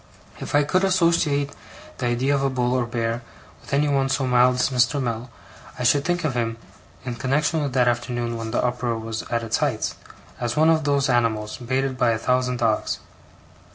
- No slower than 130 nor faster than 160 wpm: No, fast, 205 wpm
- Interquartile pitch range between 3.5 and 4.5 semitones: No, average, 3.0 semitones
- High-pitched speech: No, low, 125 Hz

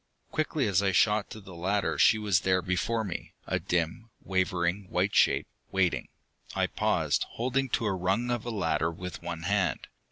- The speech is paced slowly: No, average, 180 wpm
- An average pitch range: Yes, average, 3.4 semitones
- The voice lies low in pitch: Yes, very low, 95 Hz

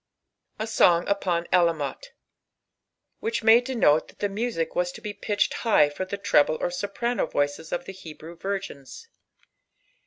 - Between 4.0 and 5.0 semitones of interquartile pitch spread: Yes, average, 4.5 semitones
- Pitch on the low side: No, medium, 185 Hz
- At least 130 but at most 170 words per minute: Yes, average, 150 wpm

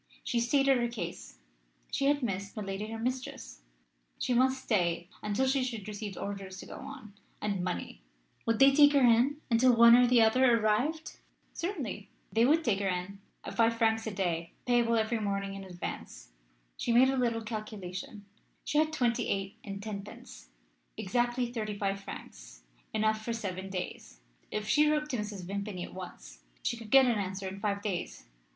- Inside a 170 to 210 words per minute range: Yes, average, 180 wpm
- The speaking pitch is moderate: No, high, 220 Hz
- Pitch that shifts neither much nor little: Yes, average, 3.9 semitones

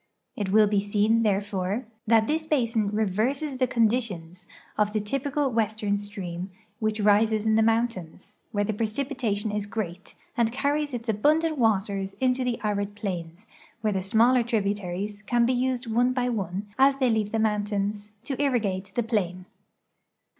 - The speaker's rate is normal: Yes, average, 160 wpm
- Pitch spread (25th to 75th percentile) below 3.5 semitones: Yes, average, 3.1 semitones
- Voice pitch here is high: Yes, high, 215 Hz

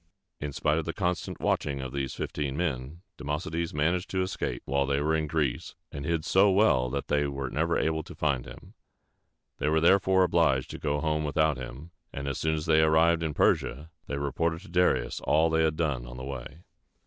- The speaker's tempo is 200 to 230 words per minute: Yes, fast, 205 wpm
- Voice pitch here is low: Yes, very low, 75 Hz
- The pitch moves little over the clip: No, average, 3.0 semitones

